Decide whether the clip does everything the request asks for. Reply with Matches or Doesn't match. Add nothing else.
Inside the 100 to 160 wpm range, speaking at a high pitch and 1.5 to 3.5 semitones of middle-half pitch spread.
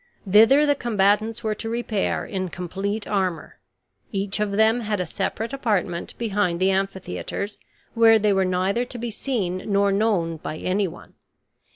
Matches